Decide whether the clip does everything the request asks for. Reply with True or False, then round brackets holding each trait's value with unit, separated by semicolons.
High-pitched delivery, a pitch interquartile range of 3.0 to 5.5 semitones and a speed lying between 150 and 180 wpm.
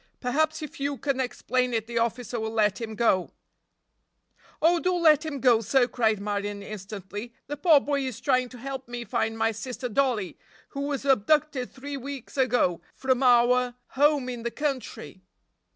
True (250 Hz; 3.7 semitones; 170 wpm)